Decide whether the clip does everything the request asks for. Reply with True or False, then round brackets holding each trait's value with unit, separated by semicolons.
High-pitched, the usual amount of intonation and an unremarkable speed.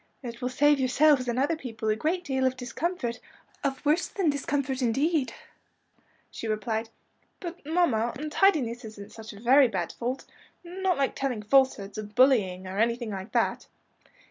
True (255 Hz; 4.6 semitones; 165 wpm)